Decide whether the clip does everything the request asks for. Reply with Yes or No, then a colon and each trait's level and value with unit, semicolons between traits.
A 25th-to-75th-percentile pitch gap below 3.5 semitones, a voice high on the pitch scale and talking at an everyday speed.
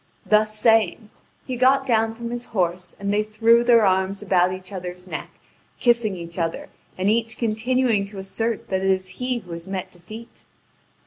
No: average, 3.8 semitones; high, 210 Hz; average, 180 wpm